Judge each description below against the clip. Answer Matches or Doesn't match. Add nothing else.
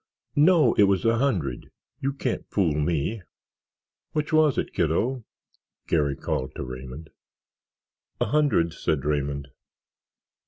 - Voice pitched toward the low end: Matches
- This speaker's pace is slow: Matches